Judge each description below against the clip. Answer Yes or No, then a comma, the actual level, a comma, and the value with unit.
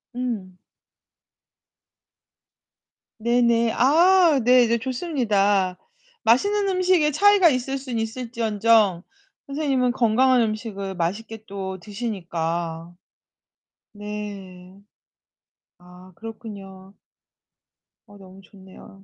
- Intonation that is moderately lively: Yes, average, 4.7 semitones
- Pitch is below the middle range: No, high, 220 Hz